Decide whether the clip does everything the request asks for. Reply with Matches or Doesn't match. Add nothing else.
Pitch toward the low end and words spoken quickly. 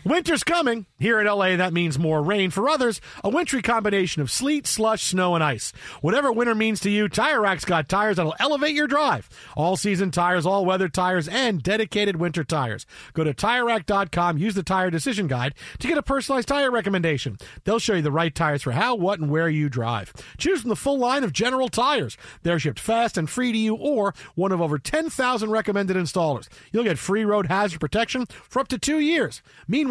Doesn't match